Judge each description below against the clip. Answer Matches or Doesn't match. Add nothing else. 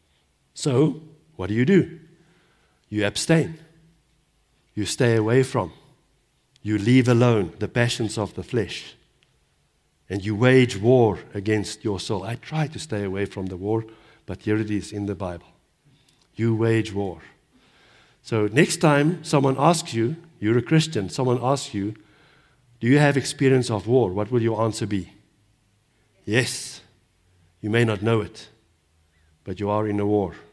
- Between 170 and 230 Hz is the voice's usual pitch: Doesn't match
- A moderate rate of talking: Matches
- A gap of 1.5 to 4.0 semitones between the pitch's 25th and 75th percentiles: Doesn't match